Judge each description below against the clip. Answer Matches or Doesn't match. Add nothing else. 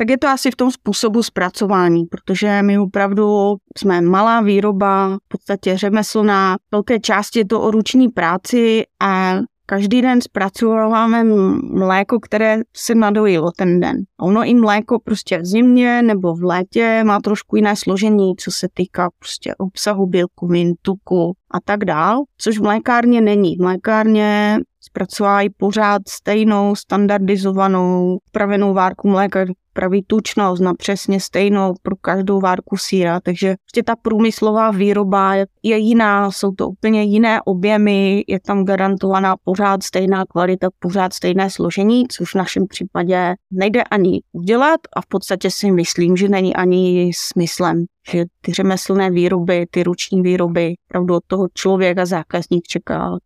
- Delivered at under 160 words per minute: Matches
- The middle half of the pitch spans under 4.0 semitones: Matches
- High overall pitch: Matches